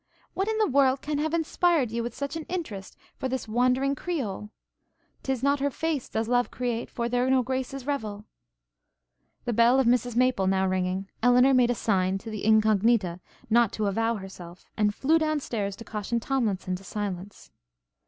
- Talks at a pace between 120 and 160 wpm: No, average, 185 wpm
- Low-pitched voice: No, high, 240 Hz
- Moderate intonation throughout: Yes, average, 4.4 semitones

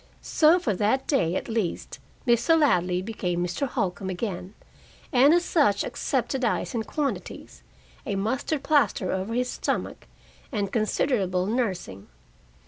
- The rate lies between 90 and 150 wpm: Yes, slow, 135 wpm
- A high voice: Yes, high, 220 Hz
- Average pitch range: No, wide, 6.0 semitones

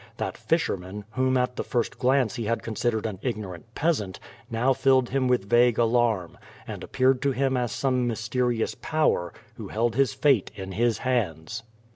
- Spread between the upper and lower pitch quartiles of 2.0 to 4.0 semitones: Yes, average, 3.2 semitones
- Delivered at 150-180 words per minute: Yes, average, 170 wpm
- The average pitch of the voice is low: Yes, low, 120 Hz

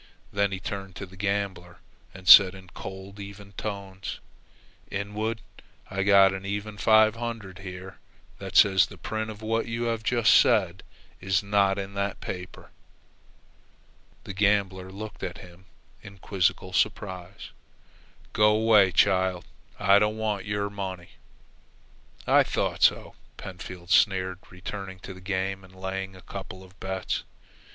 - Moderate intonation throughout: No, narrow, 1.6 semitones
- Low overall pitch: Yes, very low, 95 Hz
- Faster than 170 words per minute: No, average, 145 wpm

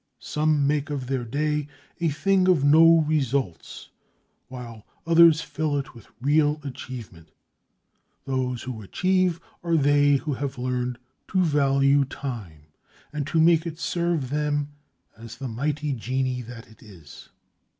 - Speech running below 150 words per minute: Yes, average, 140 wpm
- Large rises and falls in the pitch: No, average, 3.6 semitones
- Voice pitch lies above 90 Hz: Yes, medium, 140 Hz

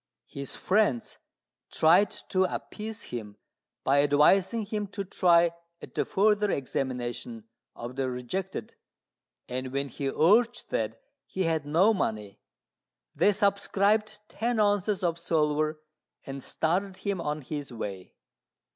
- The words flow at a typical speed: No, slow, 125 wpm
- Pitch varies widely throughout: Yes, wide, 6.8 semitones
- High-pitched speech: No, medium, 170 Hz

